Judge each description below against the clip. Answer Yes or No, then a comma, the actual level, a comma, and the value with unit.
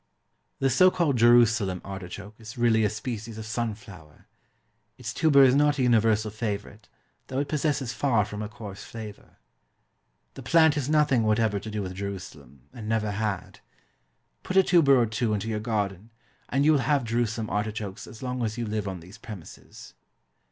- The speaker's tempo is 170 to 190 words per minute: Yes, average, 175 wpm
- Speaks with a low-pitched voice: Yes, low, 110 Hz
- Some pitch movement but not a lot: Yes, average, 3.4 semitones